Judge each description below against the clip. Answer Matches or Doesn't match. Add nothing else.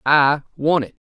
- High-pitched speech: Doesn't match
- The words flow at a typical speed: Matches